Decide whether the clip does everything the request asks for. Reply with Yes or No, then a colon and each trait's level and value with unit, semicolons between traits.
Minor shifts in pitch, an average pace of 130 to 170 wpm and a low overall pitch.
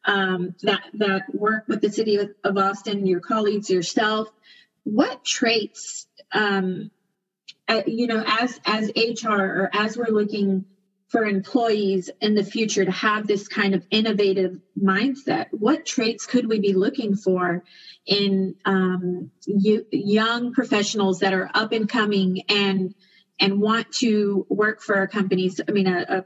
No: narrow, 2.3 semitones; average, 155 wpm; high, 205 Hz